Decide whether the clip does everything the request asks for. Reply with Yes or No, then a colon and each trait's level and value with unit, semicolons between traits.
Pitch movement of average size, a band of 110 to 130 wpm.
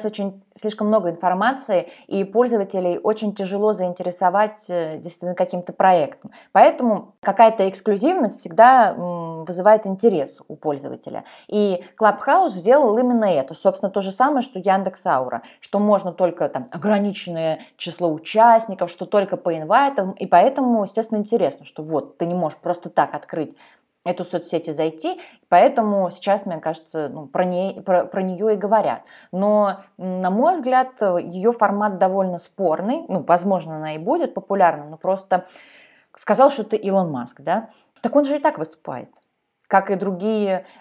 No: average, 3.3 semitones; average, 145 wpm